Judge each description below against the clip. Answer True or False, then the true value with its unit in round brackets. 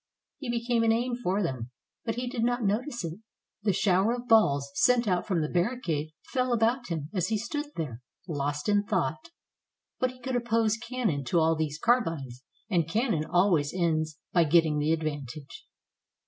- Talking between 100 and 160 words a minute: False (175 wpm)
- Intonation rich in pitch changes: True (7.2 semitones)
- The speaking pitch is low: False (190 Hz)